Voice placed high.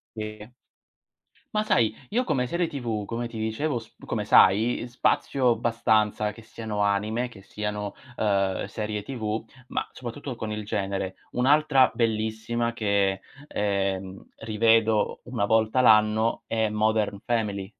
No: low, 110 Hz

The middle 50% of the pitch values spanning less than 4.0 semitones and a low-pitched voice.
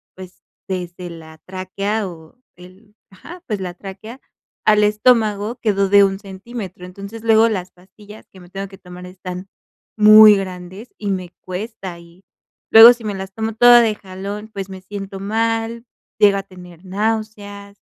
No: average, 2.7 semitones; high, 200 Hz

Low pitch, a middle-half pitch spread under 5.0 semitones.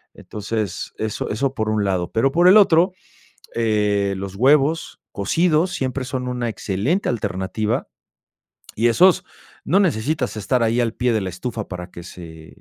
No: low, 115 Hz; wide, 5.5 semitones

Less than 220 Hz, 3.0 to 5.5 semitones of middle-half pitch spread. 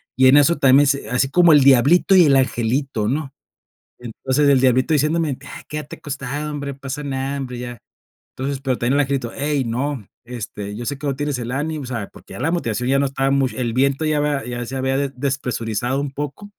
No: low, 135 Hz; narrow, 2.5 semitones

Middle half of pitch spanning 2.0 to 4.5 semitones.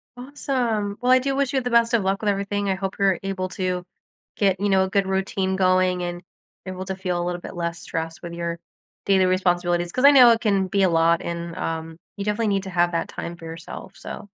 Yes: average, 2.7 semitones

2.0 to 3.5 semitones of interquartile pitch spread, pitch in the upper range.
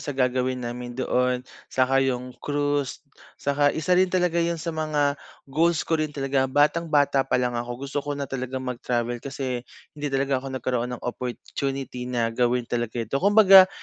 No: average, 2.7 semitones; low, 135 Hz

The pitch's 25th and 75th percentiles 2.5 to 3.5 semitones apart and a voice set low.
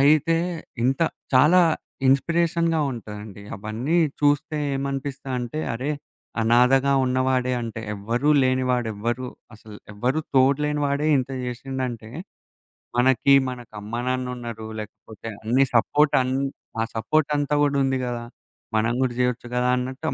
Yes: average, 2.8 semitones; low, 130 Hz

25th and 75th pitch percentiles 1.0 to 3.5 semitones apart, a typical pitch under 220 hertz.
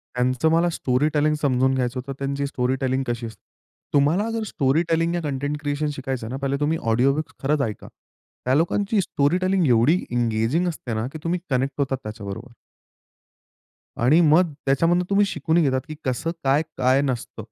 No: average, 4.2 semitones; medium, 140 Hz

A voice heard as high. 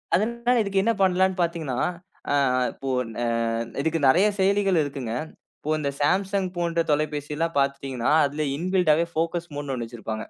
No: medium, 165 Hz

